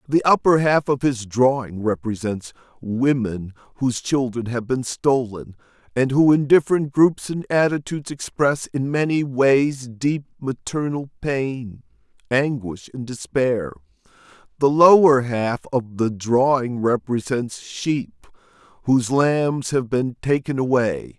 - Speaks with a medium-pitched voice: No, low, 130 Hz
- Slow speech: Yes, slow, 125 wpm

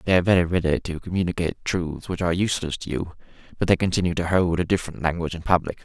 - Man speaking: Yes, male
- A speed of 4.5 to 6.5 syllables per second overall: No, 7.4 syllables/s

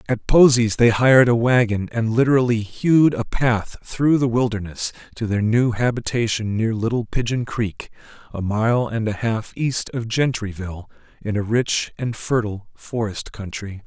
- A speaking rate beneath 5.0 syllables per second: Yes, 4.6 syllables/s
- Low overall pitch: Yes, low, 115 Hz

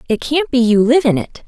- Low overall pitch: No, very high, 255 Hz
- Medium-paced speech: No, fast, 285 wpm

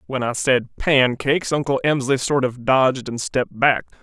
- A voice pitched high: No, low, 130 Hz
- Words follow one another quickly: No, average, 180 wpm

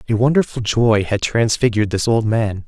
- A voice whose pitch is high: No, low, 110 Hz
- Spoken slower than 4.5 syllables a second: No, 5.3 syllables/s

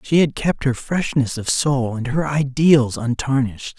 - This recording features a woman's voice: No, male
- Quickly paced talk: No, average, 175 wpm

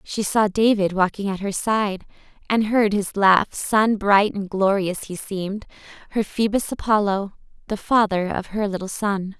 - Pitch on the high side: Yes, high, 200 Hz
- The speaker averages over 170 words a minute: No, average, 160 wpm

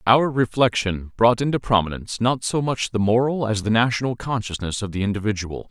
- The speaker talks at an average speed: Yes, average, 180 wpm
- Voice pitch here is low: Yes, low, 115 Hz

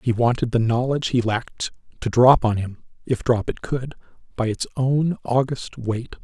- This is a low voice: Yes, low, 120 Hz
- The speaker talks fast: No, average, 185 wpm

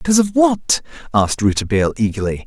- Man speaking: Yes, male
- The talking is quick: No, average, 145 wpm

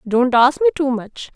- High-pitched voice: Yes, very high, 260 Hz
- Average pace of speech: No, fast, 220 wpm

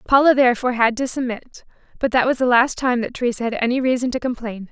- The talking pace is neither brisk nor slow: No, fast, 230 wpm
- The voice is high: Yes, high, 245 Hz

